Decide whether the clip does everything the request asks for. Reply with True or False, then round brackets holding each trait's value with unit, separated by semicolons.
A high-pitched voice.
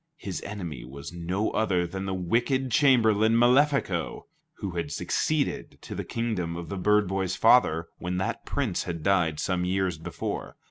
False (95 Hz)